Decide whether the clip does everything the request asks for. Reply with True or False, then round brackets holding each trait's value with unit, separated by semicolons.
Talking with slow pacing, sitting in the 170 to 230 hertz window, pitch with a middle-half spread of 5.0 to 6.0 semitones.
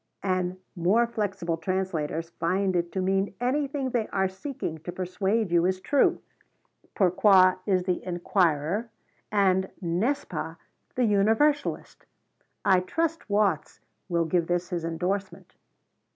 False (130 wpm; 190 Hz; 3.3 semitones)